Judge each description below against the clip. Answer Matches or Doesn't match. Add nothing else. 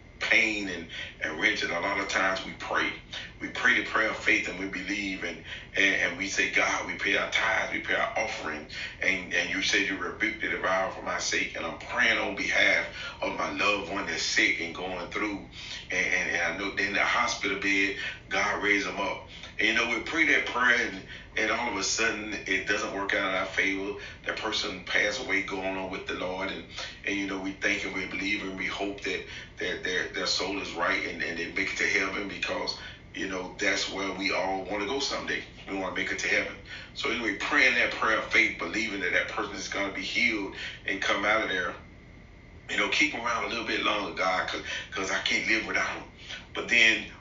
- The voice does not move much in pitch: Matches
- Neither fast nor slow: Doesn't match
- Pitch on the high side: Doesn't match